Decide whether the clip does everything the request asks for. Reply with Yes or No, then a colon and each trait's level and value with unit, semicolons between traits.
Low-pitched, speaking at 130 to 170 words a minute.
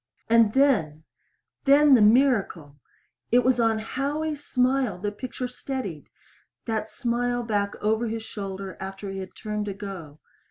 No: high, 220 Hz; average, 145 wpm